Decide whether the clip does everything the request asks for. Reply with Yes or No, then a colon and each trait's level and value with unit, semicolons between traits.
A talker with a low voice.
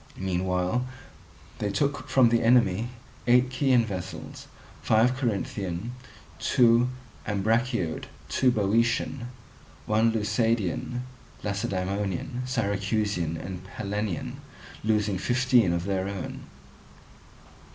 Yes: low, 105 Hz